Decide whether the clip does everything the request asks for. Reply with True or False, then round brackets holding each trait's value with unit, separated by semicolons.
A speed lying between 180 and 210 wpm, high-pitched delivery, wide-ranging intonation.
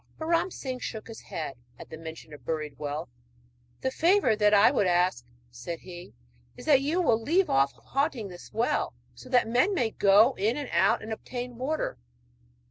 True (190 wpm; 220 Hz; 7.7 semitones)